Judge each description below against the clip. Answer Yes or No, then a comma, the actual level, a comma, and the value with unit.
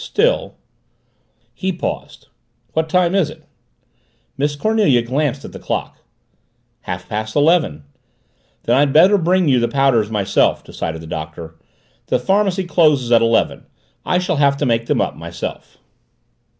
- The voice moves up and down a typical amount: No, wide, 7.5 semitones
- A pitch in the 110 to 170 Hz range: Yes, medium, 140 Hz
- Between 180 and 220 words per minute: No, average, 150 wpm